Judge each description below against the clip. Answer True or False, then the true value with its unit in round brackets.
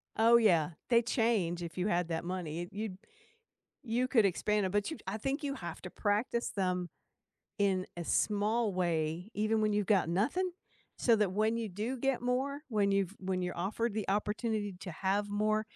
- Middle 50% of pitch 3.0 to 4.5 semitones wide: True (3.7 semitones)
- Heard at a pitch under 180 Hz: False (205 Hz)